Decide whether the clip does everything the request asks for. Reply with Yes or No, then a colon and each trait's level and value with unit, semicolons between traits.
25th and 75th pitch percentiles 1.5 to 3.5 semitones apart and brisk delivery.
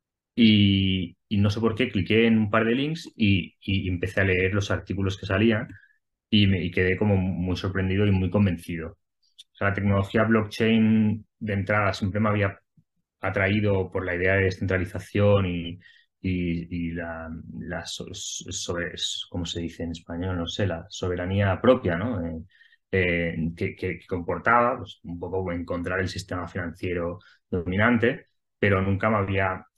No: average, 2.8 semitones; average, 165 wpm